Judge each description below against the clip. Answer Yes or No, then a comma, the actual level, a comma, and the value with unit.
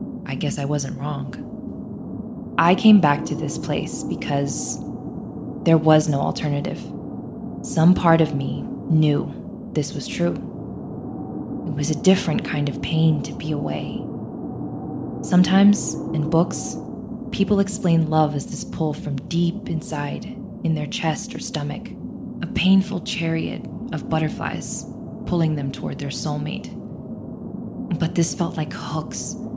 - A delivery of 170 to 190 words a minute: No, slow, 135 wpm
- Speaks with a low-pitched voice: No, medium, 165 Hz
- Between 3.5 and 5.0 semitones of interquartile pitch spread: Yes, average, 4.5 semitones